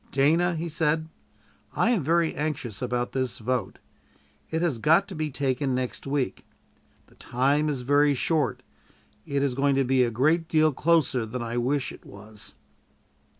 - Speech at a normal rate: Yes, average, 165 wpm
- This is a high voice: No, medium, 140 Hz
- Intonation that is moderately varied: Yes, average, 3.7 semitones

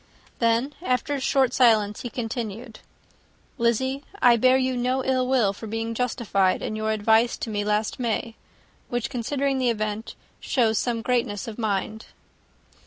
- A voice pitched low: No, high, 235 Hz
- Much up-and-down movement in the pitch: No, average, 2.7 semitones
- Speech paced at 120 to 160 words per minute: Yes, average, 155 wpm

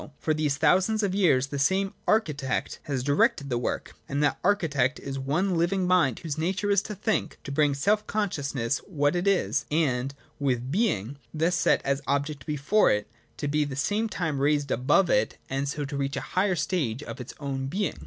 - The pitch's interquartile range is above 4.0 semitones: Yes, average, 5.1 semitones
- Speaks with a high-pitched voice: No, medium, 150 Hz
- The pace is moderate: No, fast, 210 wpm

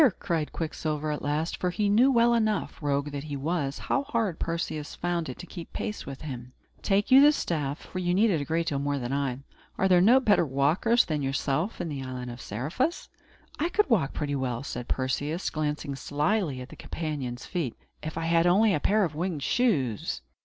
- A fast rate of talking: Yes, fast, 210 wpm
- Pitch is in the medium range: Yes, medium, 155 Hz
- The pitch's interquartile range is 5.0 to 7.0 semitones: Yes, wide, 5.6 semitones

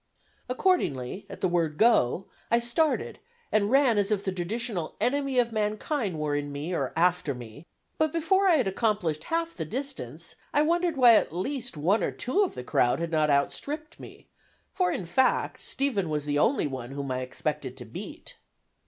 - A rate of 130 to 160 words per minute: No, average, 185 wpm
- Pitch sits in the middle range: No, high, 200 Hz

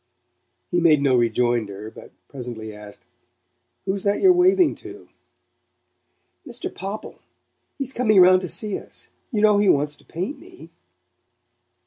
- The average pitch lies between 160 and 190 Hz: Yes, medium, 185 Hz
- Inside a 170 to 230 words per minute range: No, slow, 135 wpm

